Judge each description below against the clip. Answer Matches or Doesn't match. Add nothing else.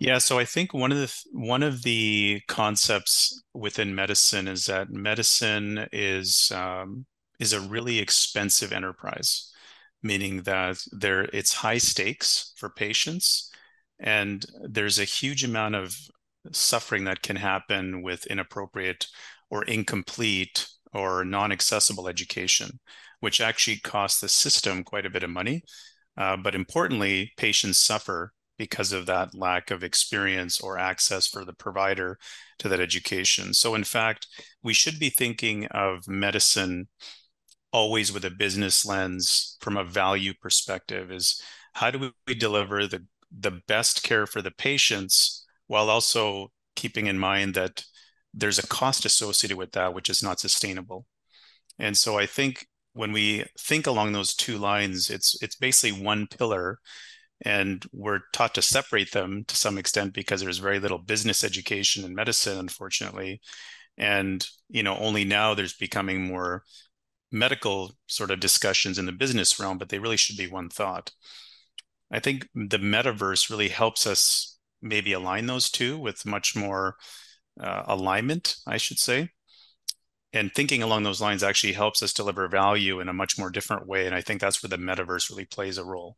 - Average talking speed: Matches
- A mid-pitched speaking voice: Doesn't match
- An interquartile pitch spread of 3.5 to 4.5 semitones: Doesn't match